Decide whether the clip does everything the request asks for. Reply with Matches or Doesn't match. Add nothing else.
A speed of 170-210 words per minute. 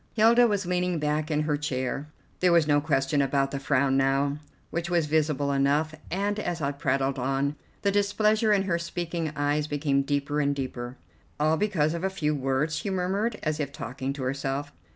Matches